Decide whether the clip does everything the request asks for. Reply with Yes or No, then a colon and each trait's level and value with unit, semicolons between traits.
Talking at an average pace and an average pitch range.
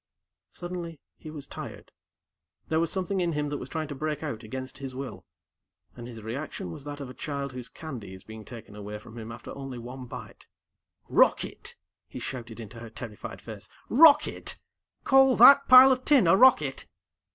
No: average, 185 wpm; wide, 6.2 semitones